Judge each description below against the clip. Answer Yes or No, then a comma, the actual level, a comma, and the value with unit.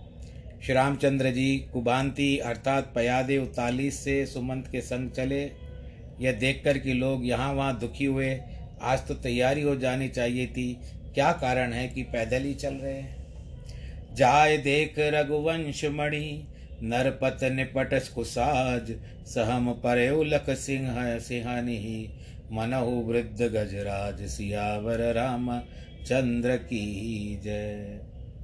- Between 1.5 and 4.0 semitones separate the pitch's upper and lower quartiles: Yes, average, 2.7 semitones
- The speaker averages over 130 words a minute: No, average, 115 wpm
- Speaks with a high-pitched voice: No, low, 125 Hz